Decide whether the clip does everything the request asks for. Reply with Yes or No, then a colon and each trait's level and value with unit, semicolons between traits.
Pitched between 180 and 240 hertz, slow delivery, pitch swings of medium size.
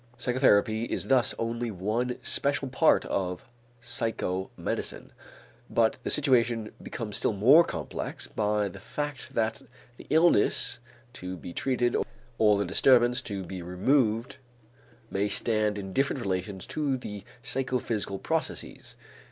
No: low, 115 Hz; slow, 125 wpm; average, 4.0 semitones